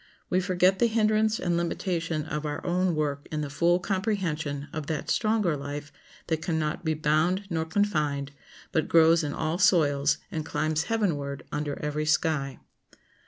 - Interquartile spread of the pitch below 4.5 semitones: Yes, average, 3.3 semitones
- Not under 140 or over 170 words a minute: Yes, average, 165 wpm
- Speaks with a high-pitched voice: No, medium, 160 Hz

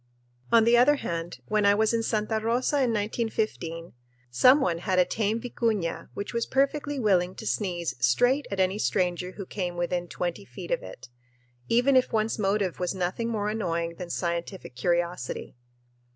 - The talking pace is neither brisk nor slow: Yes, average, 170 wpm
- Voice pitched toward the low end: No, high, 205 Hz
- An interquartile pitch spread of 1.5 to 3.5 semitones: No, average, 4.7 semitones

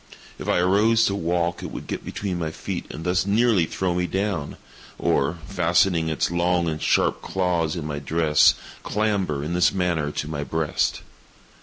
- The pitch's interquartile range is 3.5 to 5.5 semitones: No, average, 3.1 semitones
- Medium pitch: No, very low, 85 Hz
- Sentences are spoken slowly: No, average, 175 wpm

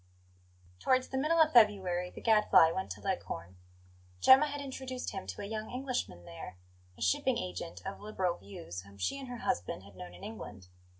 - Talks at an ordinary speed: Yes, average, 185 wpm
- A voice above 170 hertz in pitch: Yes, medium, 185 Hz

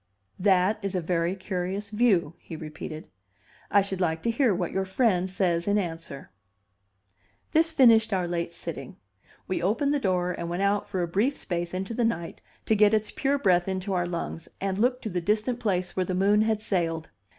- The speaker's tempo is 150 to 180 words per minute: No, average, 195 wpm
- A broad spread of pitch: No, average, 3.6 semitones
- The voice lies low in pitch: No, high, 190 Hz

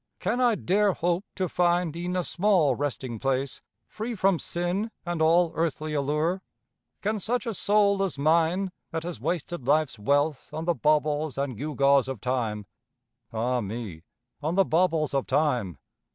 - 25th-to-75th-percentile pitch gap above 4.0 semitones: Yes, average, 4.7 semitones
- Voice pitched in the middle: Yes, medium, 160 Hz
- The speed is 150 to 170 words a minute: Yes, average, 160 wpm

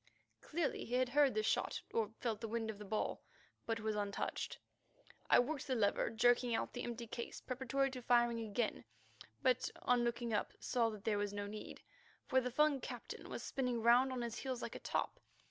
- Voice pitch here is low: No, high, 240 Hz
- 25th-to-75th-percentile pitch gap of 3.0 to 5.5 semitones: No, narrow, 2.6 semitones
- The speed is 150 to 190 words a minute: No, average, 200 wpm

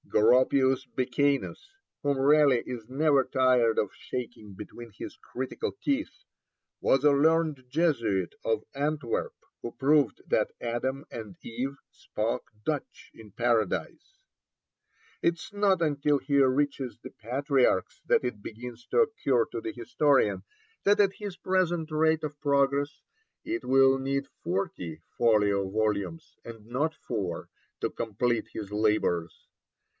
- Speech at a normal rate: No, slow, 130 wpm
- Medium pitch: No, low, 130 Hz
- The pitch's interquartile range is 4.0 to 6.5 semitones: Yes, average, 4.7 semitones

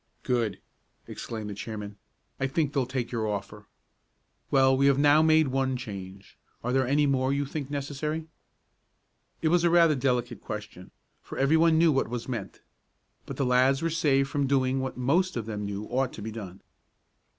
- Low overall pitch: Yes, low, 130 Hz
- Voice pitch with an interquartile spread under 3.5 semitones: No, average, 4.0 semitones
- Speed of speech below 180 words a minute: No, average, 185 wpm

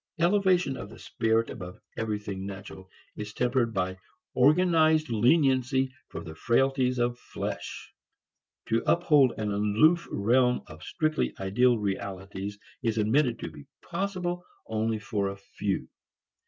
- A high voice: No, low, 115 Hz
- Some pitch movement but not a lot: No, wide, 5.8 semitones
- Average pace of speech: No, slow, 125 wpm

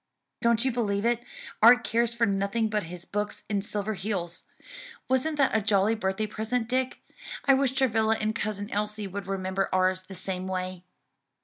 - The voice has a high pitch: Yes, high, 210 Hz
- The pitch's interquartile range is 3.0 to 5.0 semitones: Yes, average, 3.3 semitones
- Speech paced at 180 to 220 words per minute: No, average, 170 wpm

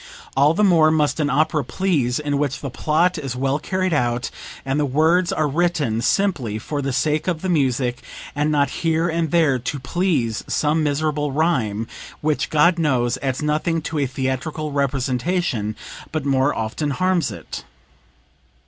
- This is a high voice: No, medium, 150 Hz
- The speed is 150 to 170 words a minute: Yes, average, 165 wpm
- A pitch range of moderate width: Yes, average, 3.5 semitones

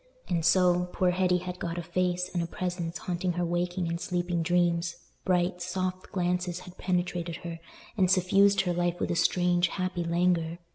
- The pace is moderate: Yes, average, 180 wpm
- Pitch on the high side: No, medium, 180 Hz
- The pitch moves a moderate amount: No, narrow, 0.9 semitones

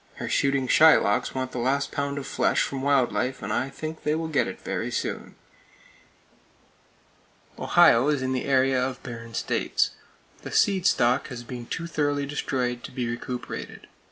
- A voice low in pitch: Yes, low, 130 Hz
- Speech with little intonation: Yes, narrow, 2.3 semitones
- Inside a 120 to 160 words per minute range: No, average, 170 wpm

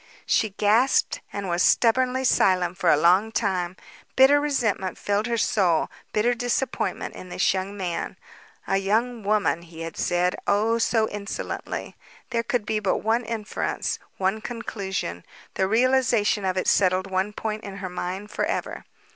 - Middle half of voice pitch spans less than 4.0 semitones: Yes, average, 3.6 semitones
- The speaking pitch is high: Yes, high, 205 Hz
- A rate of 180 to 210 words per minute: No, average, 155 wpm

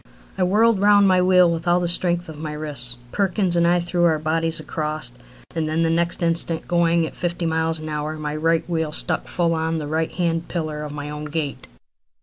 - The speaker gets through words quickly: Yes, fast, 220 wpm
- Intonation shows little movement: Yes, narrow, 1.9 semitones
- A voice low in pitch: No, medium, 165 Hz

